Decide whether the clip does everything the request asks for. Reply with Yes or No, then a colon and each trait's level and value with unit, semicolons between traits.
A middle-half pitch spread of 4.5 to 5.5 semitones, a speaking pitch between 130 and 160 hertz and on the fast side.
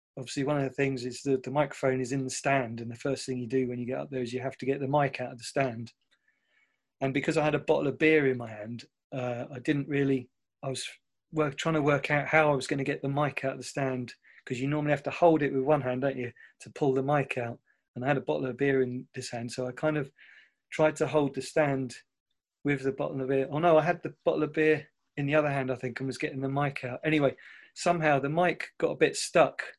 No: narrow, 2.4 semitones; low, 135 Hz; fast, 280 wpm